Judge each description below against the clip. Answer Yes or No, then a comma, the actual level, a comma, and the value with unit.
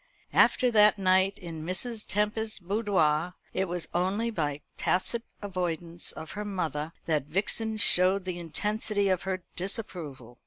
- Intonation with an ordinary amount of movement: Yes, average, 3.8 semitones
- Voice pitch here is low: No, medium, 185 Hz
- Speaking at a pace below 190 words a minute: Yes, average, 140 wpm